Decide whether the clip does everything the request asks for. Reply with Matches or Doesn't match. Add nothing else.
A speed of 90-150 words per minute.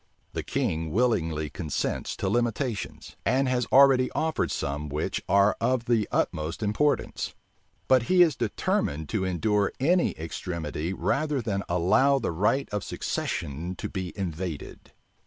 Matches